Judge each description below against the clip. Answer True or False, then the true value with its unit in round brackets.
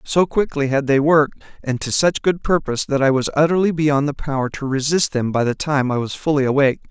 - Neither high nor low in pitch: True (145 Hz)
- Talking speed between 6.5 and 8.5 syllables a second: False (5.9 syllables/s)